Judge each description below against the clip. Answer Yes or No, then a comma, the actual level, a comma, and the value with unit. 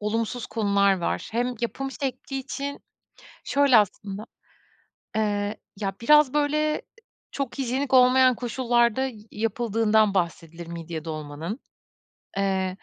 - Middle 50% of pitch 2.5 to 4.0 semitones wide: No, average, 4.9 semitones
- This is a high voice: Yes, high, 225 Hz